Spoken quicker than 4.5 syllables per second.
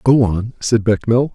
Yes: 5.0 syllables/s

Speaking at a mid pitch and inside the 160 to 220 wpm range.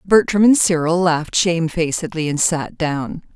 No: medium, 170 Hz; average, 145 wpm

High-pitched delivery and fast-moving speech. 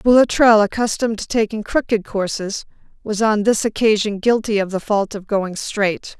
No: high, 210 Hz; average, 165 wpm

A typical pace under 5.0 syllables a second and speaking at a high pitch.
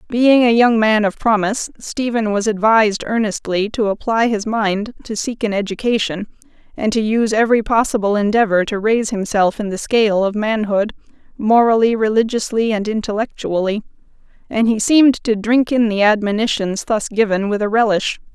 No: 5.3 syllables/s; high, 215 Hz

